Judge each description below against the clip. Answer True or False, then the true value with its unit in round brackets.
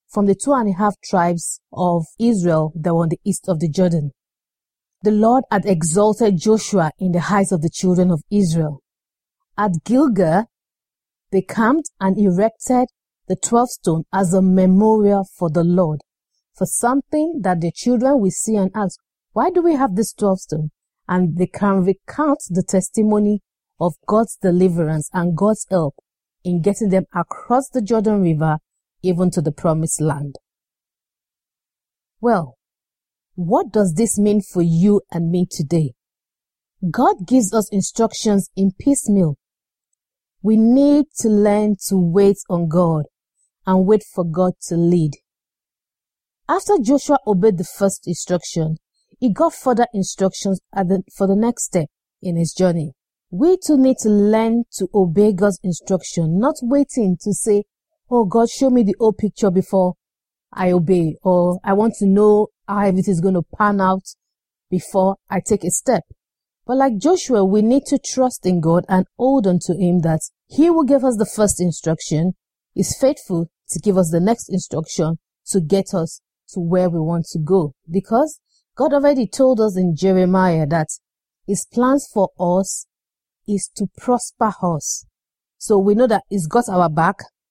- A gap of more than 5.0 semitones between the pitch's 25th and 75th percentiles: False (3.8 semitones)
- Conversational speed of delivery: True (165 wpm)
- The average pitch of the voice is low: False (195 Hz)